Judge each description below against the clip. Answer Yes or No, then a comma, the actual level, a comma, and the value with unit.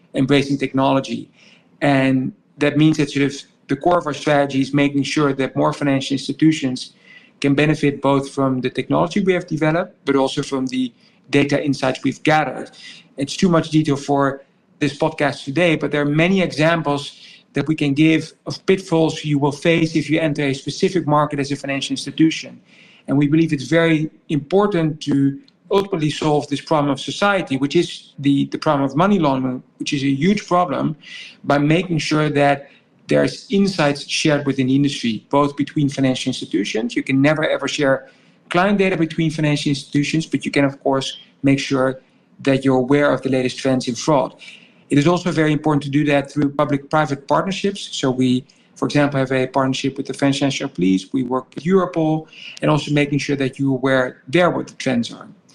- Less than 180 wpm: No, fast, 190 wpm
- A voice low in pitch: No, medium, 145 Hz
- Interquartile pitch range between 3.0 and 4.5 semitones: No, narrow, 2.6 semitones